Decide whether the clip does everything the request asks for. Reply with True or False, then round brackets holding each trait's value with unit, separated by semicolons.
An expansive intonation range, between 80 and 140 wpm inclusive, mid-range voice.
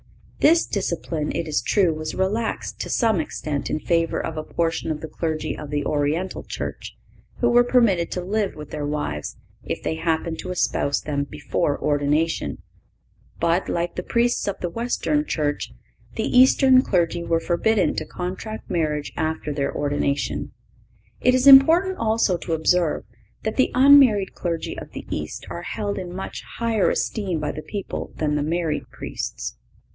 False (6.0 semitones; 165 wpm; 170 Hz)